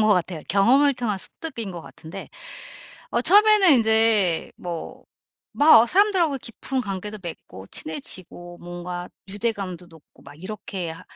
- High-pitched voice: Yes, high, 200 Hz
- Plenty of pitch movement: Yes, wide, 5.7 semitones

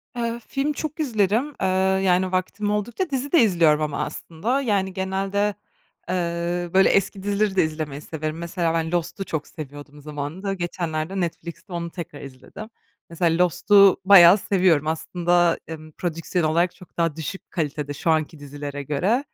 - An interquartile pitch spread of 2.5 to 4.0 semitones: Yes, average, 3.7 semitones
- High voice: No, medium, 175 Hz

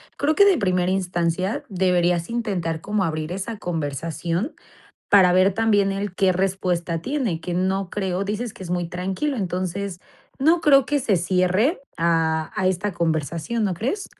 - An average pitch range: Yes, average, 3.2 semitones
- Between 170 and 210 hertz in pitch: Yes, medium, 185 Hz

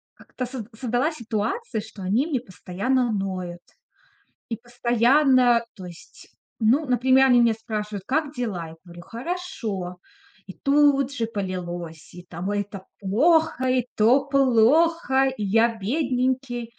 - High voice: Yes, high, 235 Hz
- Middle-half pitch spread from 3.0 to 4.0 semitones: No, average, 4.7 semitones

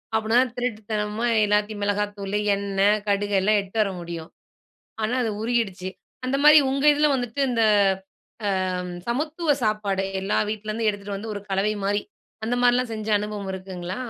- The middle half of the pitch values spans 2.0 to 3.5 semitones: Yes, average, 2.7 semitones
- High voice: Yes, high, 210 Hz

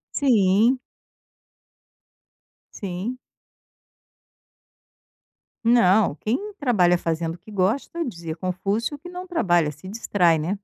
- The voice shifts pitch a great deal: Yes, wide, 5.9 semitones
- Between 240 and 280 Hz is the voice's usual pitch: No, high, 195 Hz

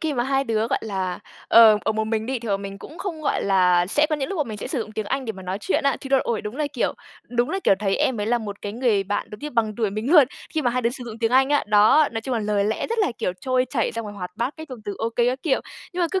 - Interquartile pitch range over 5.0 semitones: No, average, 4.3 semitones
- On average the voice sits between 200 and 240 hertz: Yes, high, 230 Hz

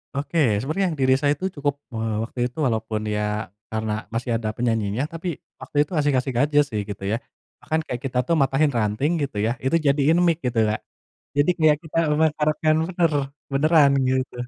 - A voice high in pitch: No, medium, 140 Hz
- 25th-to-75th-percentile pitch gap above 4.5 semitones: Yes, average, 5.0 semitones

